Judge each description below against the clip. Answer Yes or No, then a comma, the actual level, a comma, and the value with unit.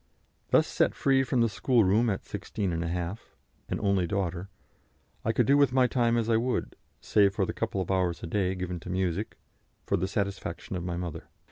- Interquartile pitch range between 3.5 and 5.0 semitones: Yes, average, 4.4 semitones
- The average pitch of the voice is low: Yes, low, 100 Hz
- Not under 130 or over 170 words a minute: No, average, 195 wpm